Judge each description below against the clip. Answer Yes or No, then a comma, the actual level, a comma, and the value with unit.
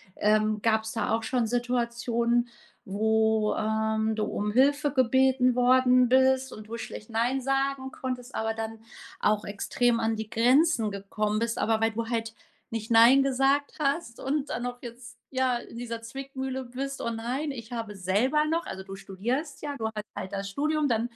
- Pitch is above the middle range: Yes, high, 235 Hz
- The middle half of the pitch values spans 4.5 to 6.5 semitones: No, average, 3.1 semitones